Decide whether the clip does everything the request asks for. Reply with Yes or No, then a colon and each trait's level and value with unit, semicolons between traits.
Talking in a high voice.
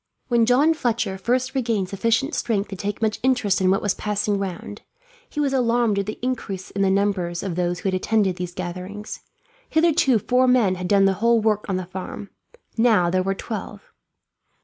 Yes: high, 205 Hz